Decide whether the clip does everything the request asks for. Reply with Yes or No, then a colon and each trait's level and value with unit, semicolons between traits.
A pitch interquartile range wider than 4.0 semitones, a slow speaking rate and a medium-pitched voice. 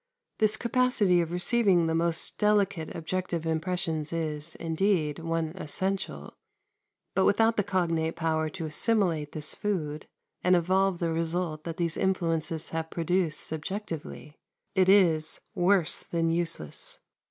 No: average, 3.0 semitones; slow, 130 wpm; medium, 170 Hz